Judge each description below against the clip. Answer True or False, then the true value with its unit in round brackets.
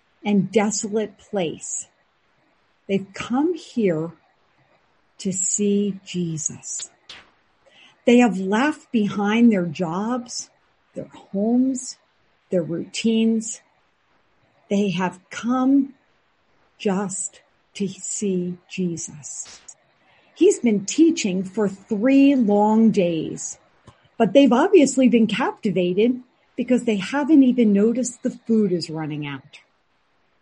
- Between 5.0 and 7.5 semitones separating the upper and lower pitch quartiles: False (4.6 semitones)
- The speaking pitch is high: True (215 Hz)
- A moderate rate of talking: False (95 wpm)